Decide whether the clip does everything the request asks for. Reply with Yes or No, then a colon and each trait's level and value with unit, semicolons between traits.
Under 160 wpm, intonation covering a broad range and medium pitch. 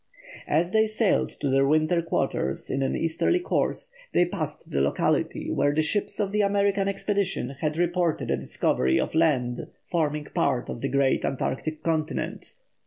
No: average, 165 wpm; wide, 6.0 semitones; medium, 160 Hz